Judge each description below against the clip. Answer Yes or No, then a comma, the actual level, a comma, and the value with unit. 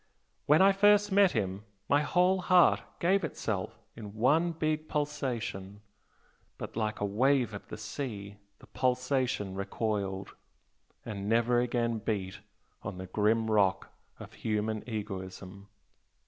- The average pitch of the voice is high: No, low, 110 Hz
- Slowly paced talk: Yes, slow, 130 wpm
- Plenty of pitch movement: Yes, wide, 6.1 semitones